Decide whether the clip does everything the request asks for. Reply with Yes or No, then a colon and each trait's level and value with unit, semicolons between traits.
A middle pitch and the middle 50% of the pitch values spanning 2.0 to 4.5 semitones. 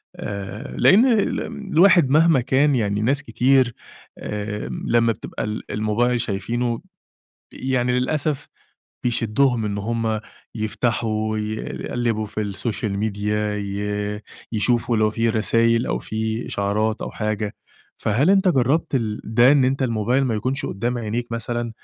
No: low, 115 Hz; average, 3.1 semitones